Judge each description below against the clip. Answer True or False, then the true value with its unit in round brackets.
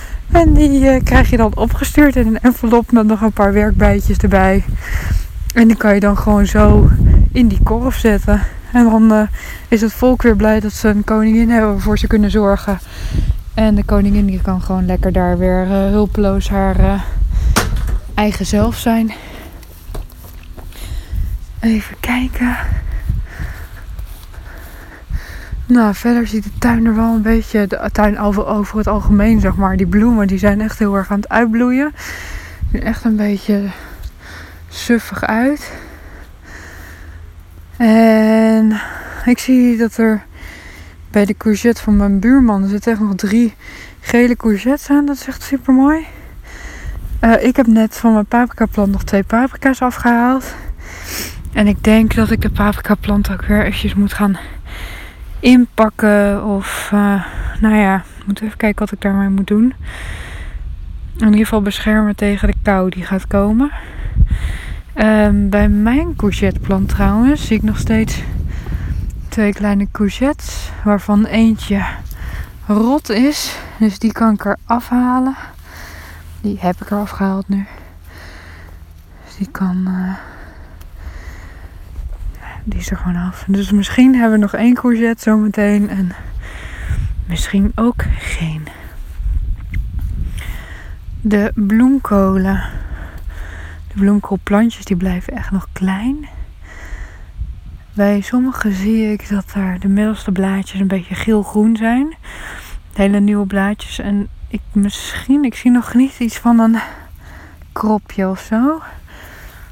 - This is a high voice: True (205 Hz)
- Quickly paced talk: False (140 wpm)